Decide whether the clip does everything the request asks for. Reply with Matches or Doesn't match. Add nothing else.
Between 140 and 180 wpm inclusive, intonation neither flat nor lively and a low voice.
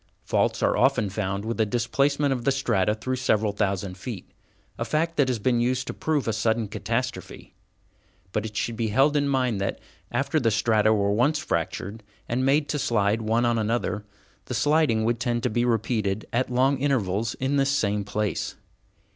Doesn't match